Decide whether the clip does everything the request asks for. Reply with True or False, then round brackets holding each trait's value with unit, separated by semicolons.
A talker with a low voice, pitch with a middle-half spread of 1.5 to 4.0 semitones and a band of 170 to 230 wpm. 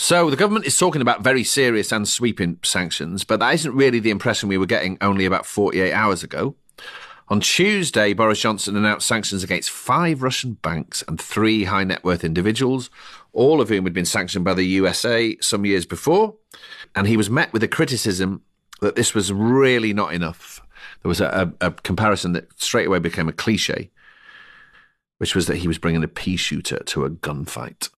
False (105 Hz; 5.6 semitones; 195 wpm)